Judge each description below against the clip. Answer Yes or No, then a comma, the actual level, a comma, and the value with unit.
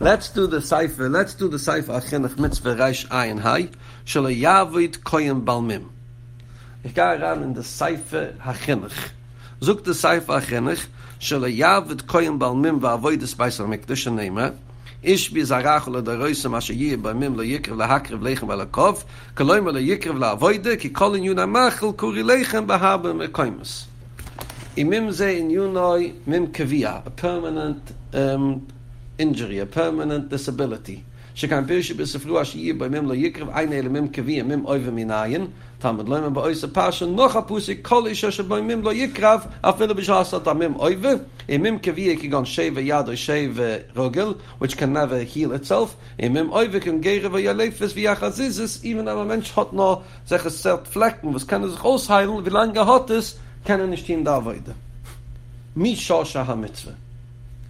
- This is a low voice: No, medium, 145 Hz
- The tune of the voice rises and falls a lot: Yes, wide, 7.2 semitones